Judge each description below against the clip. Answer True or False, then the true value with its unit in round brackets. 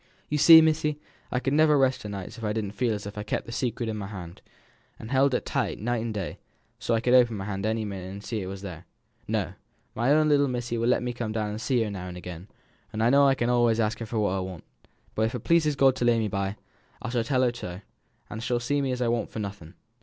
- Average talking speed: False (285 wpm)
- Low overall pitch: True (115 Hz)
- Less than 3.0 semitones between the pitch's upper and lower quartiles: False (3.6 semitones)